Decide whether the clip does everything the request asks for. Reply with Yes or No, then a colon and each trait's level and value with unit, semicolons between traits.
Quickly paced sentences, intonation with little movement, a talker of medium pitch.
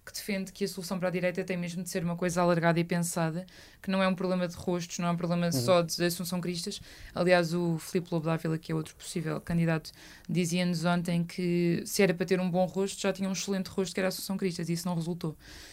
Yes: fast, 250 wpm; narrow, 1.7 semitones; medium, 180 Hz